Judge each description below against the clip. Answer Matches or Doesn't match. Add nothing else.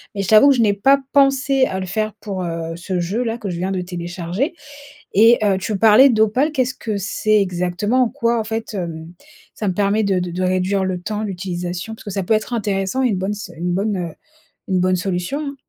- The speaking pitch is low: Doesn't match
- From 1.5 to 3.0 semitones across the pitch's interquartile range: Doesn't match